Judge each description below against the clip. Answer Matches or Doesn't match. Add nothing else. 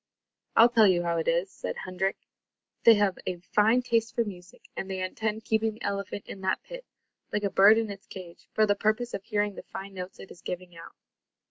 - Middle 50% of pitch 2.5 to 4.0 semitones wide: Matches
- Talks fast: Matches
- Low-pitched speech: Doesn't match